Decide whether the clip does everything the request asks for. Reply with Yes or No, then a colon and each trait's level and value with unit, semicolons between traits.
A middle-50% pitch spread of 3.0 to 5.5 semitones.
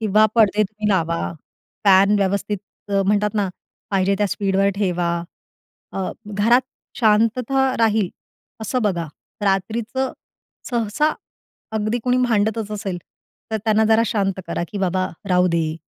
No: narrow, 2.4 semitones